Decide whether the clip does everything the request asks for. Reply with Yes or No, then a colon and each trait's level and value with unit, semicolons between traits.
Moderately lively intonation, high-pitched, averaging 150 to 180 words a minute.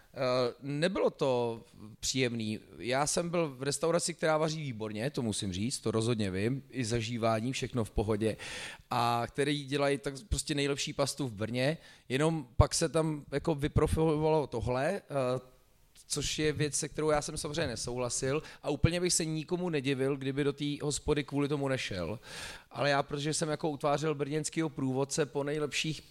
No: average, 3.8 semitones; medium, 140 Hz; average, 160 wpm